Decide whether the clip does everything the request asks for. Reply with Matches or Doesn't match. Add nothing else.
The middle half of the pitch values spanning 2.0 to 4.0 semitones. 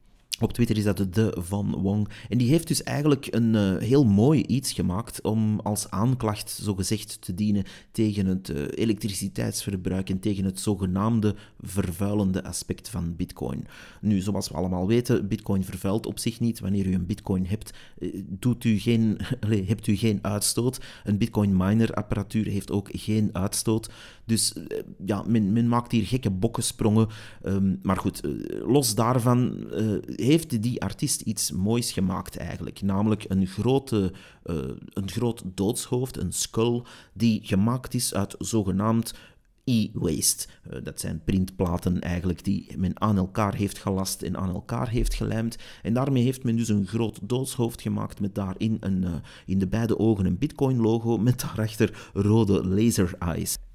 Matches